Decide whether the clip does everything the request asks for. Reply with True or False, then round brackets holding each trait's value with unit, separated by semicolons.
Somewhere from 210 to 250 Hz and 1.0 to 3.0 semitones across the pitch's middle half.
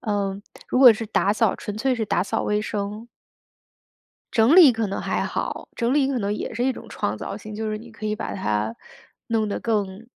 True (215 Hz; 2.5 semitones)